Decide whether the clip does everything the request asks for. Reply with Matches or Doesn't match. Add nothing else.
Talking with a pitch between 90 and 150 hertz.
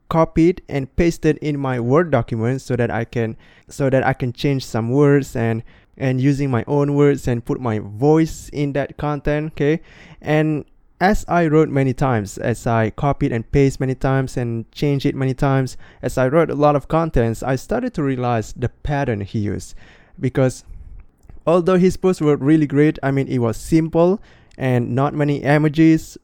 Matches